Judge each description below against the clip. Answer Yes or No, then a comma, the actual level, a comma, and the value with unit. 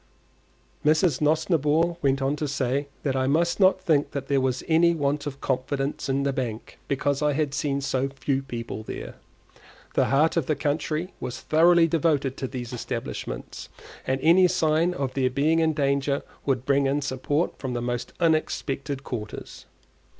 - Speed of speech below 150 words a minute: No, average, 165 wpm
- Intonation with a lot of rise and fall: No, average, 2.8 semitones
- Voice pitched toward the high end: No, medium, 140 Hz